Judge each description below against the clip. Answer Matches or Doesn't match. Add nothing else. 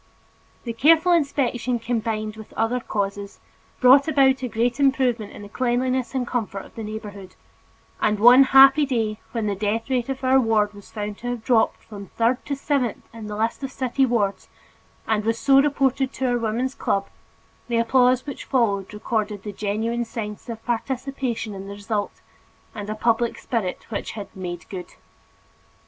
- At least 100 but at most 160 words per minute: Doesn't match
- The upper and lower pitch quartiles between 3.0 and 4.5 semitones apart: Matches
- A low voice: Doesn't match